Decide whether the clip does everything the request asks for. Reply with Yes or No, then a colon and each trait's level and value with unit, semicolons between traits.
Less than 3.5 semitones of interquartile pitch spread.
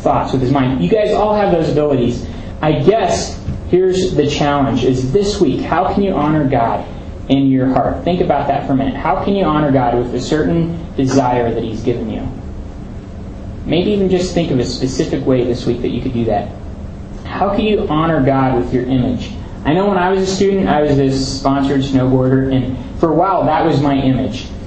No: average, 4.3 semitones